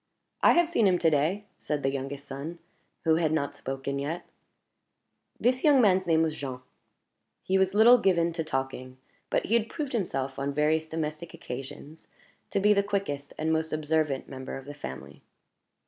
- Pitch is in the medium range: Yes, medium, 160 Hz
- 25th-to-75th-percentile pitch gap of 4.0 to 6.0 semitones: Yes, wide, 5.4 semitones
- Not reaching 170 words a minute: No, average, 180 wpm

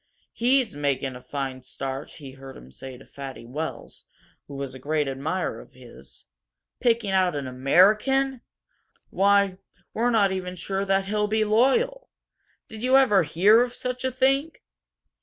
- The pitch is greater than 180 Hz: Yes, high, 190 Hz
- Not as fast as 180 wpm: Yes, average, 160 wpm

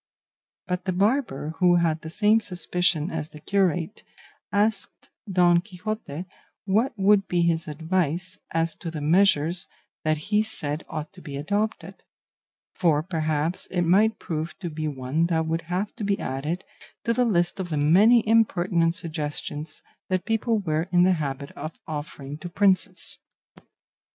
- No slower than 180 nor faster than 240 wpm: No, average, 155 wpm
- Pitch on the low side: No, medium, 175 Hz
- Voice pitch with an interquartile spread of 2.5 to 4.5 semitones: Yes, average, 4.0 semitones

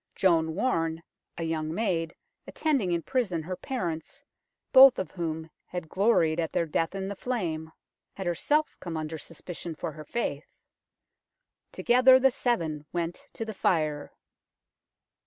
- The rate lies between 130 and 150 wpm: Yes, average, 140 wpm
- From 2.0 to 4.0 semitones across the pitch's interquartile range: No, wide, 5.5 semitones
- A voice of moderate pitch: Yes, medium, 170 Hz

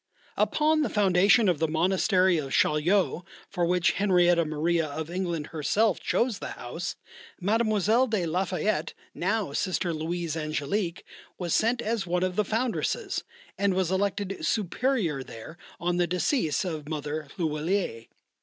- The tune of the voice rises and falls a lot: No, average, 4.2 semitones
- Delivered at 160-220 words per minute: No, average, 145 wpm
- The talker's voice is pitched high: No, medium, 180 Hz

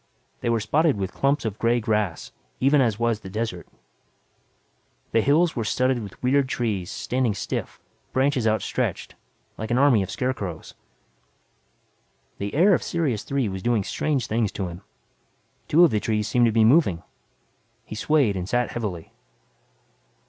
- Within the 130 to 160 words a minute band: Yes, average, 155 wpm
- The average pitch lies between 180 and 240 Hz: No, low, 115 Hz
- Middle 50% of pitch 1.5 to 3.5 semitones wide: No, average, 4.2 semitones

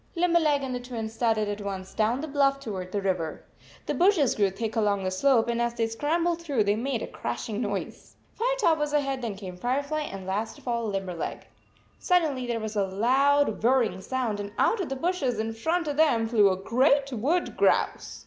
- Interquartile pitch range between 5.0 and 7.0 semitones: Yes, wide, 5.5 semitones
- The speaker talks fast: Yes, fast, 210 wpm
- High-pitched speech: Yes, high, 235 Hz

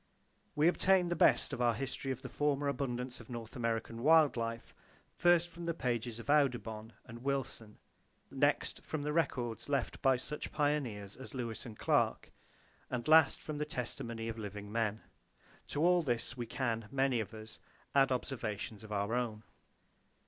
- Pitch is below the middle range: Yes, low, 125 Hz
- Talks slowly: No, average, 170 wpm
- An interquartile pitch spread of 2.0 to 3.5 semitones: No, average, 4.1 semitones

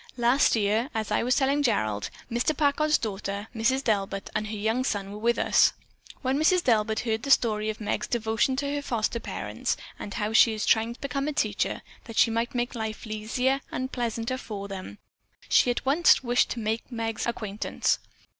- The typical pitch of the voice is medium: No, high, 230 Hz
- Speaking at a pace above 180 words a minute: Yes, average, 190 wpm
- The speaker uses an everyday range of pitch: Yes, average, 3.3 semitones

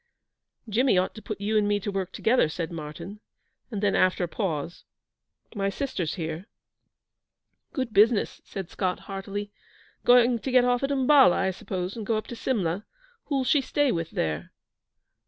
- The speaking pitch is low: No, high, 205 Hz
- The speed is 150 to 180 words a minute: Yes, average, 170 wpm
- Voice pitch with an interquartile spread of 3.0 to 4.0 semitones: No, average, 5.1 semitones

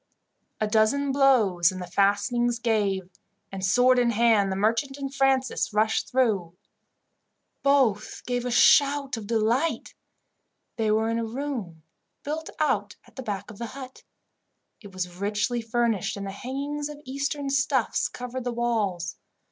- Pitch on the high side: Yes, high, 235 Hz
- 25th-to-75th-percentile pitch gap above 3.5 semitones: Yes, average, 4.6 semitones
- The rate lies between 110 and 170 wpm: Yes, average, 150 wpm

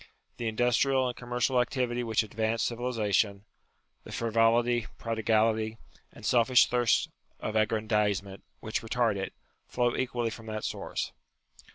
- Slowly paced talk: Yes, slow, 125 wpm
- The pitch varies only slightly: Yes, narrow, 2.0 semitones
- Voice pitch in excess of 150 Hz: No, low, 115 Hz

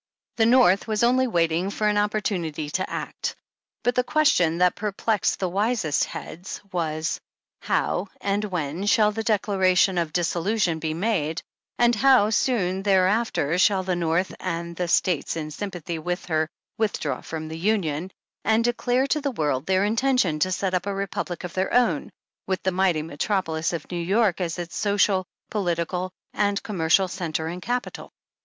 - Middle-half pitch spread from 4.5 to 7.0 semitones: No, average, 4.0 semitones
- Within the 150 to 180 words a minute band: Yes, average, 170 wpm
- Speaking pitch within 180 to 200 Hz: Yes, medium, 185 Hz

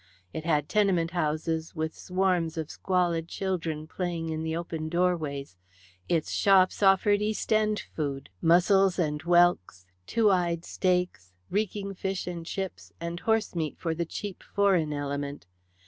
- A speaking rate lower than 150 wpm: Yes, average, 140 wpm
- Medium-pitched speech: Yes, medium, 170 Hz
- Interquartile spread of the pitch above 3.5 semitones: No, average, 3.2 semitones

